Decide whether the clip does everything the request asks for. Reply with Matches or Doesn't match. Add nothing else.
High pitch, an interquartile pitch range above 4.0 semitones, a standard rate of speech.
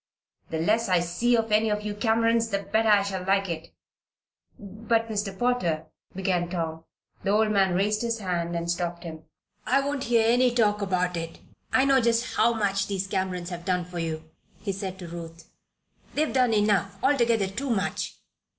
Matches